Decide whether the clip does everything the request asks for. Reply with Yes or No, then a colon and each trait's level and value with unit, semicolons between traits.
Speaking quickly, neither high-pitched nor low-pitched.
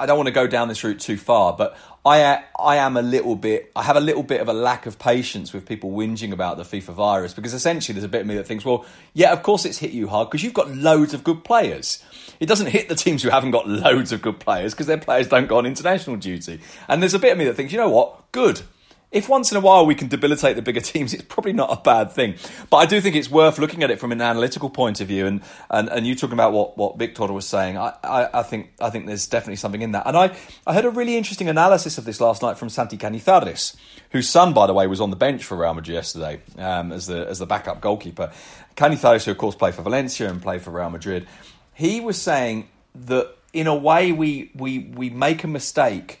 No: fast, 265 wpm; low, 125 Hz